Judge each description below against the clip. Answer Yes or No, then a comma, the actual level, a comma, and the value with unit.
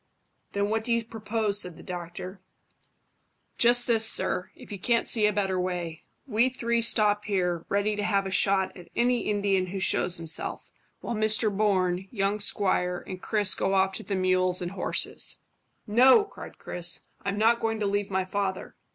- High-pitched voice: Yes, high, 200 Hz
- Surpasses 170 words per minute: Yes, average, 180 wpm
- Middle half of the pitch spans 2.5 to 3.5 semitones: Yes, average, 2.8 semitones